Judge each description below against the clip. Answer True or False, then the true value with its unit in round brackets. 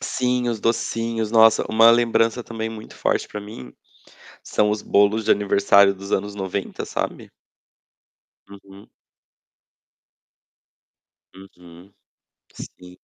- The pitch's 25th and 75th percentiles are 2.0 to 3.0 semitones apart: True (2.5 semitones)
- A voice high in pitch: False (105 Hz)